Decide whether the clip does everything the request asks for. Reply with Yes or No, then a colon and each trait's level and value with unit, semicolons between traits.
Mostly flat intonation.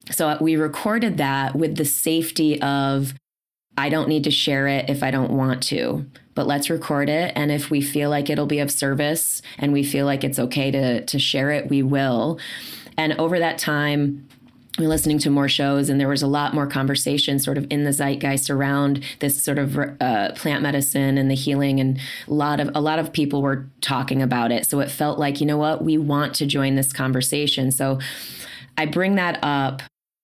Yes: narrow, 1.5 semitones